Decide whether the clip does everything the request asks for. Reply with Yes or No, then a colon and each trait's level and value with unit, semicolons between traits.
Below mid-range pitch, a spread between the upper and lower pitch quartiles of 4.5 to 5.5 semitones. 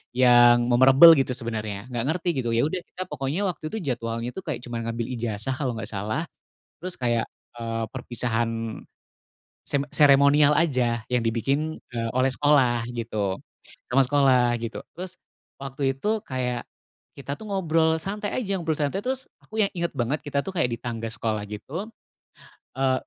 Yes: low, 130 Hz; average, 5.0 semitones